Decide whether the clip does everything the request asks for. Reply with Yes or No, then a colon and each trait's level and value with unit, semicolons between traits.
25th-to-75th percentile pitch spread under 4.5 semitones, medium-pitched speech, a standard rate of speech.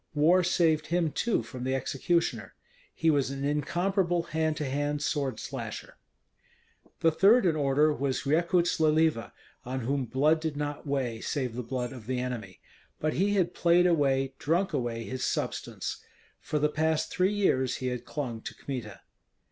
Yes: average, 4.1 semitones; medium, 145 Hz; average, 165 wpm